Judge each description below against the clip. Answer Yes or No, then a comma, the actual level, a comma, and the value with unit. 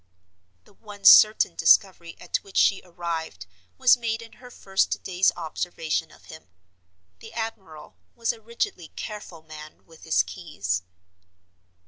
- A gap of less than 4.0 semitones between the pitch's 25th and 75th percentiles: No, average, 5.0 semitones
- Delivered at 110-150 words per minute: Yes, slow, 135 wpm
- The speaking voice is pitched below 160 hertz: No, medium, 180 Hz